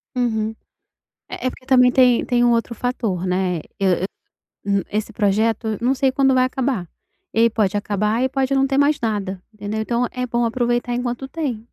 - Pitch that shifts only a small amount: No, average, 3.1 semitones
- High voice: Yes, high, 235 Hz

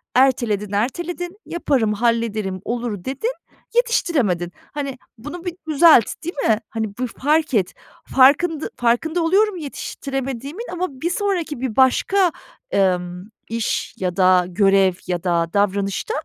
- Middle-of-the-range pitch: No, very high, 255 Hz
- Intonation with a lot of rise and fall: Yes, wide, 8.3 semitones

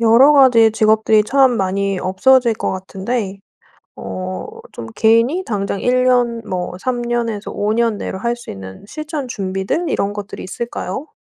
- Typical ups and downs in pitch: Yes, average, 4.1 semitones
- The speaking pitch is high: Yes, high, 220 Hz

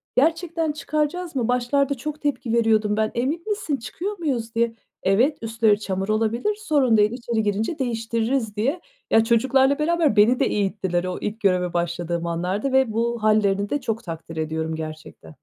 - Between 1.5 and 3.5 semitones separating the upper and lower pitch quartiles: No, average, 5.3 semitones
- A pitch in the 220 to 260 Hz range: Yes, high, 225 Hz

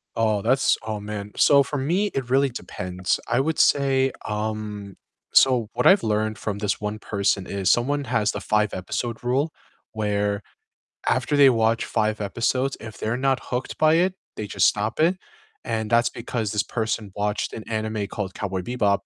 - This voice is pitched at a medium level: No, low, 110 Hz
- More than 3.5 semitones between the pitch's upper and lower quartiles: Yes, average, 3.9 semitones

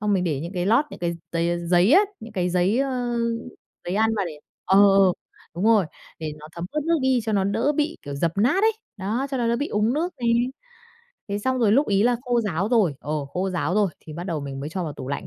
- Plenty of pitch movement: Yes, wide, 5.7 semitones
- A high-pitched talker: Yes, high, 200 Hz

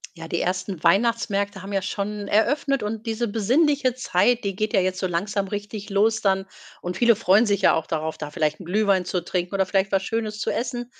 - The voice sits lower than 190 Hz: No, high, 200 Hz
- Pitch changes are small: No, average, 3.2 semitones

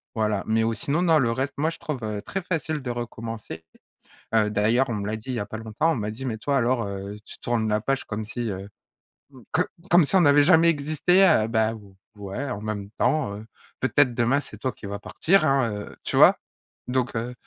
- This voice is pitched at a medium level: No, low, 120 Hz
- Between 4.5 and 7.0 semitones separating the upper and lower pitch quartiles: Yes, average, 4.9 semitones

